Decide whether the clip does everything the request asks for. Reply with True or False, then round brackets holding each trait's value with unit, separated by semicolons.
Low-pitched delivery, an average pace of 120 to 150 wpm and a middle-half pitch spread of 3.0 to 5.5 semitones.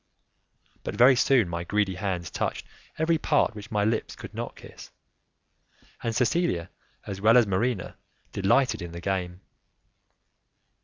True (105 Hz; 140 wpm; 5.1 semitones)